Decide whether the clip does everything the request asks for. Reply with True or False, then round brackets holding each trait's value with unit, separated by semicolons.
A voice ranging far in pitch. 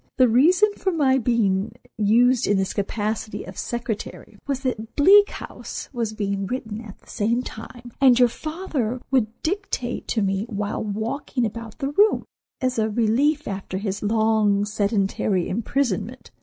False (4.0 semitones)